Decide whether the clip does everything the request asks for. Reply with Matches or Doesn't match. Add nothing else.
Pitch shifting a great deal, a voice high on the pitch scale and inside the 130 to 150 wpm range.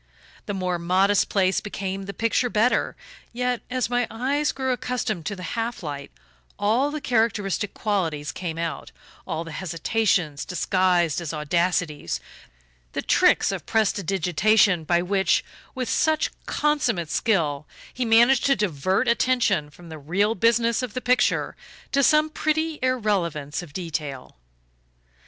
Matches